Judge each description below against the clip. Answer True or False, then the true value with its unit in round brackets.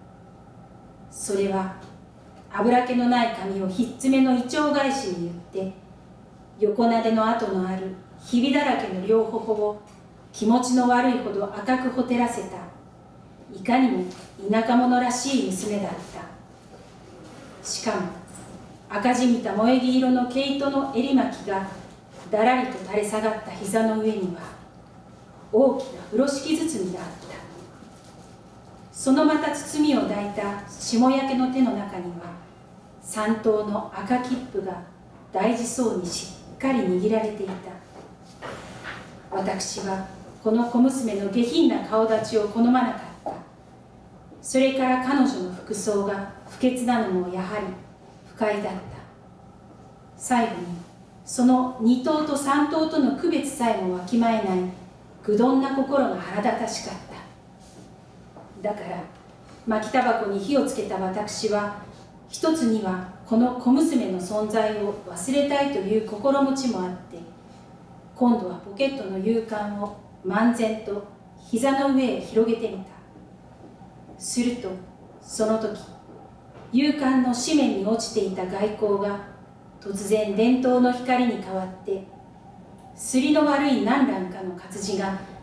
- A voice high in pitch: True (220 Hz)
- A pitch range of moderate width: True (4.4 semitones)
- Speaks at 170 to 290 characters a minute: True (240 characters per minute)